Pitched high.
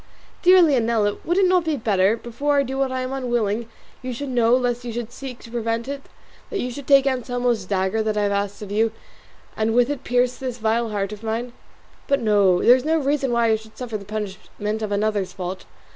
Yes: high, 235 Hz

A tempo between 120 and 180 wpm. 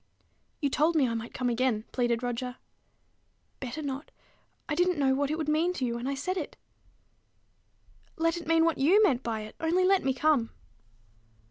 No: average, 190 wpm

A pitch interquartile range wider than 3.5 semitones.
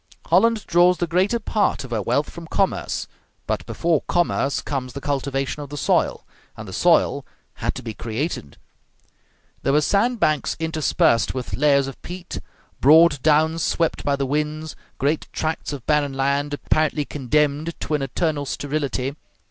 No: average, 2.9 semitones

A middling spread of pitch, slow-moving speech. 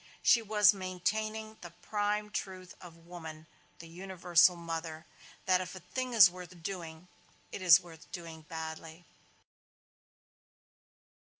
Yes: average, 3.1 semitones; slow, 120 wpm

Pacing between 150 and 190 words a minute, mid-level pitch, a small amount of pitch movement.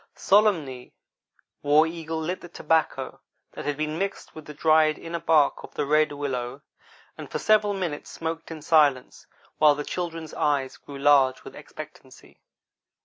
Yes: average, 155 wpm; medium, 155 Hz; narrow, 2.3 semitones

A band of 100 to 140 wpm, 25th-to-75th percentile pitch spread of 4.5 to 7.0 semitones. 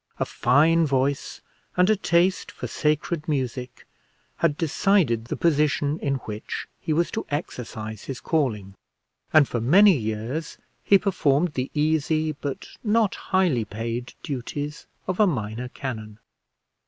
Yes: slow, 135 wpm; average, 5.2 semitones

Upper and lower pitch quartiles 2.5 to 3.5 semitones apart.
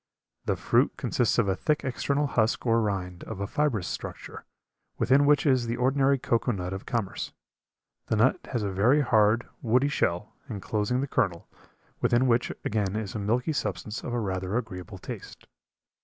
No: average, 4.5 semitones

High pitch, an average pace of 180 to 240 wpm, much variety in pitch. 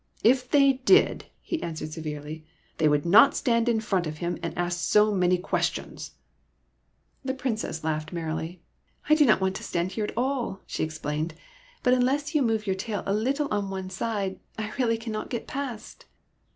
Yes: high, 210 Hz; average, 195 wpm; wide, 6.5 semitones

